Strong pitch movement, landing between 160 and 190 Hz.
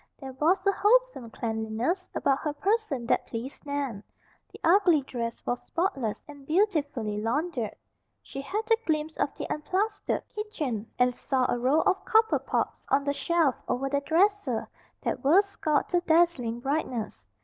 No: wide, 6.7 semitones; very high, 290 Hz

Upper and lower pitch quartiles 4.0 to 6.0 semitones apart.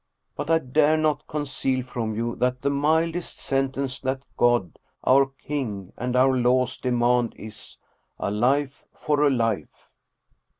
No: average, 2.9 semitones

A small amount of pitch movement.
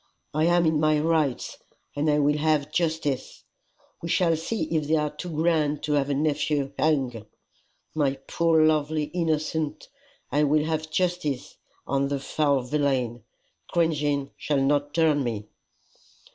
Yes: narrow, 2.0 semitones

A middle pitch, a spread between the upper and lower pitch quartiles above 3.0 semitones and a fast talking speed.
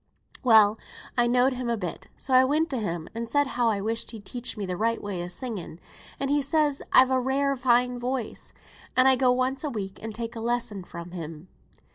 No: high, 240 Hz; average, 3.9 semitones; fast, 220 wpm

